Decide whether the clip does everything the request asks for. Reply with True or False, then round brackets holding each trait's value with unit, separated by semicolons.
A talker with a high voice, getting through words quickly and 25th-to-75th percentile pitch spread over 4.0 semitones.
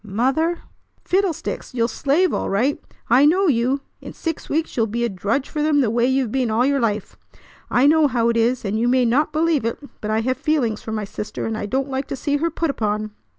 True (255 Hz; 235 wpm; 4.6 semitones)